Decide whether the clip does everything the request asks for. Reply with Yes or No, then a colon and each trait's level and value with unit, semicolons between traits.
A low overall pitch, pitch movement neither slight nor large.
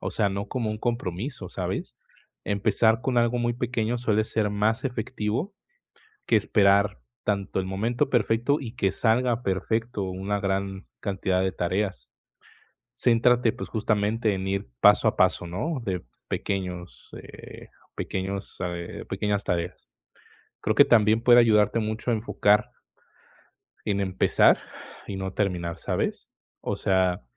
Yes: low, 105 Hz; average, 3.3 semitones